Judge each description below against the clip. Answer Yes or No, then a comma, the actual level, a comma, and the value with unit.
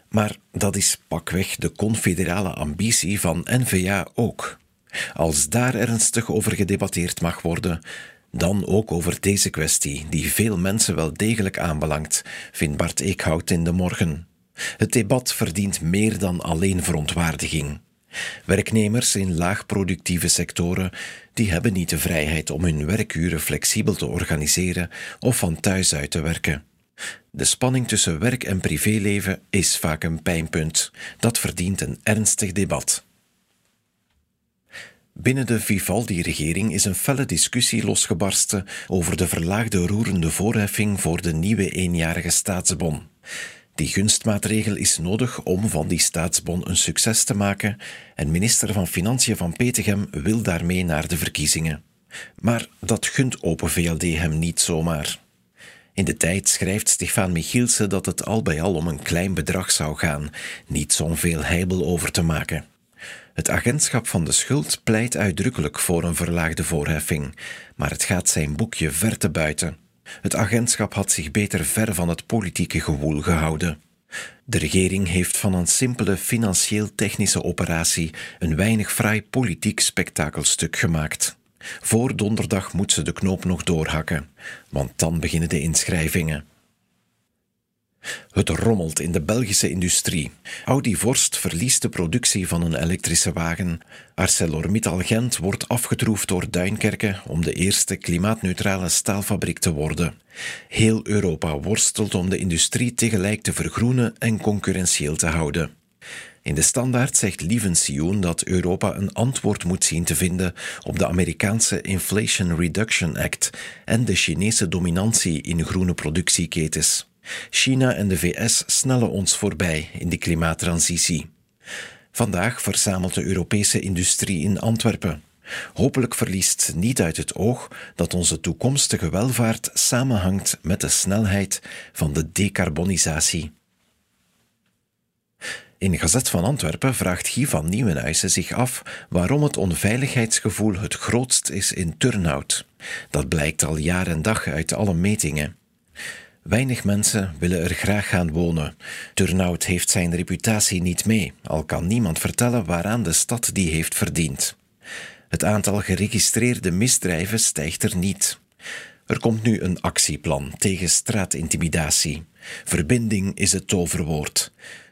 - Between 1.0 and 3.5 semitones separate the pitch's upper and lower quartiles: No, average, 4.2 semitones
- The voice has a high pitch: No, very low, 95 Hz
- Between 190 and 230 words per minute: No, slow, 135 wpm